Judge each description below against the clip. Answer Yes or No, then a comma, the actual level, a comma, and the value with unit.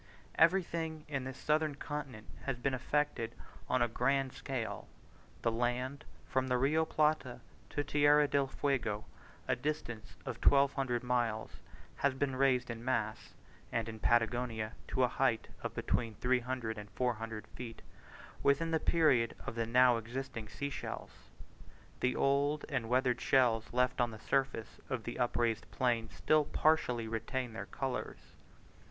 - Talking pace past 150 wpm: No, average, 145 wpm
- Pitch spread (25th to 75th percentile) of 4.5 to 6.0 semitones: No, average, 3.3 semitones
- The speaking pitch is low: Yes, low, 125 Hz